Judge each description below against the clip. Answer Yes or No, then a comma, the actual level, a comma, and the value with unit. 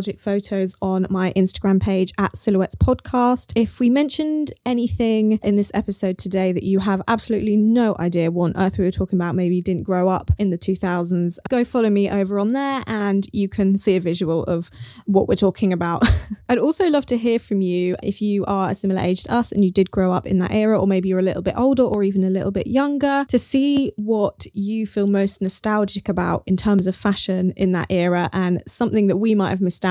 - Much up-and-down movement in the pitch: No, average, 2.7 semitones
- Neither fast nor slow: No, fast, 225 wpm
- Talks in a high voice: Yes, high, 195 Hz